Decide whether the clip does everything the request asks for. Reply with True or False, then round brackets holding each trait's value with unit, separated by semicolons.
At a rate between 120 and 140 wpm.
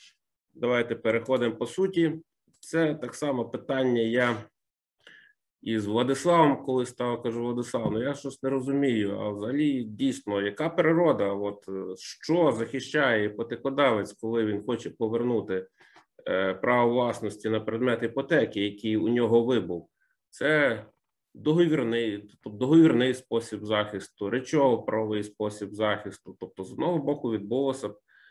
True (125 wpm)